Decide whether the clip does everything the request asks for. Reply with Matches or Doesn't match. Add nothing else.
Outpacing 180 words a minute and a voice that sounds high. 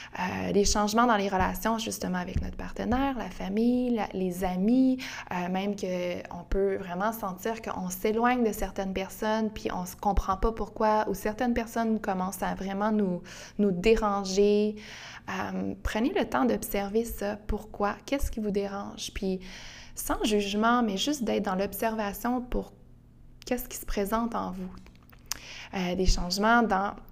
Doesn't match